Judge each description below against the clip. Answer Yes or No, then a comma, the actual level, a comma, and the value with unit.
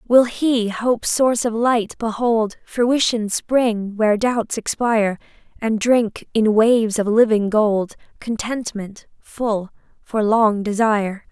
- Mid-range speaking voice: No, high, 220 Hz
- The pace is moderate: No, slow, 125 wpm